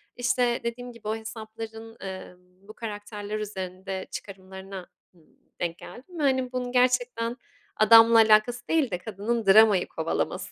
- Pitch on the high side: Yes, high, 220 Hz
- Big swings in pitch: No, average, 3.8 semitones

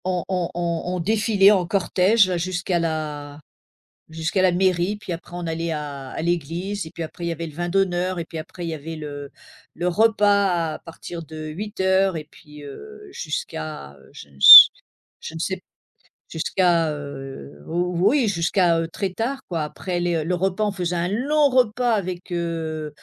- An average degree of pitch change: Yes, average, 3.1 semitones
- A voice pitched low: No, medium, 175 Hz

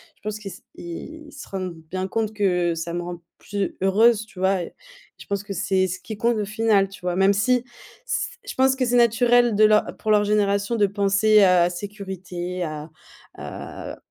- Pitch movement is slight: No, average, 3.0 semitones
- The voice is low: No, high, 200 Hz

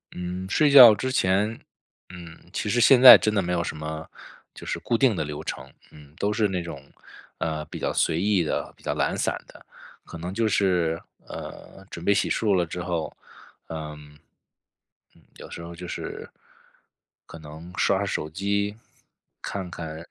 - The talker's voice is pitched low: Yes, very low, 90 Hz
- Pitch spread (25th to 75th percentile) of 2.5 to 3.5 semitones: No, average, 3.9 semitones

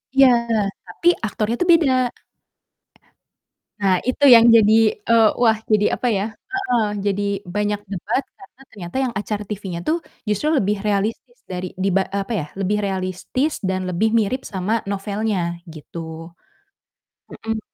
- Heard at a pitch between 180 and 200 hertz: No, high, 210 Hz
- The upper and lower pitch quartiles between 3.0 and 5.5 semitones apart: Yes, average, 3.4 semitones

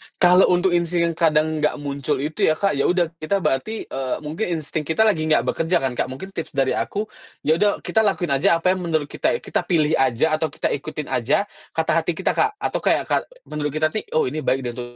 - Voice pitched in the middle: Yes, medium, 160 Hz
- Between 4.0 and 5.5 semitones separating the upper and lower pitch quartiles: No, average, 3.4 semitones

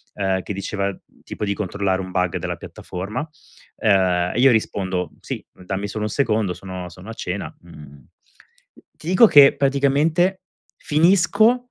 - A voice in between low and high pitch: No, low, 100 Hz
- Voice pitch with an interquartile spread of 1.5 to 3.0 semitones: No, wide, 7.2 semitones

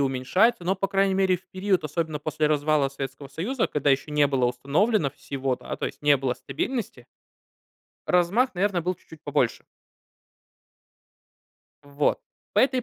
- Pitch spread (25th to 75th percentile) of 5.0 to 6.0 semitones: Yes, wide, 5.6 semitones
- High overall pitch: No, medium, 155 Hz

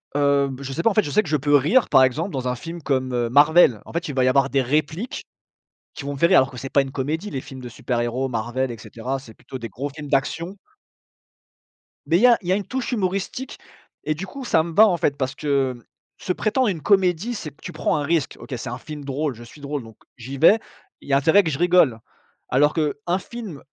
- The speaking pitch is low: No, medium, 145 Hz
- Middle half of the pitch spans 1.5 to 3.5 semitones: No, average, 4.8 semitones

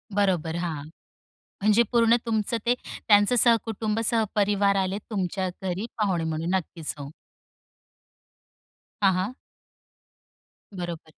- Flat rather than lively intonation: No, average, 3.8 semitones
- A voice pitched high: Yes, high, 195 Hz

